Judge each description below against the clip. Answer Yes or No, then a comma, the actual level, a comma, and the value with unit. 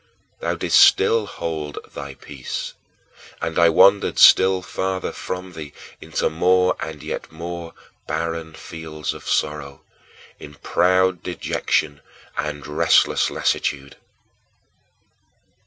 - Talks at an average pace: No, slow, 105 wpm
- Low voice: Yes, very low, 80 Hz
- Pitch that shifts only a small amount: No, average, 3.4 semitones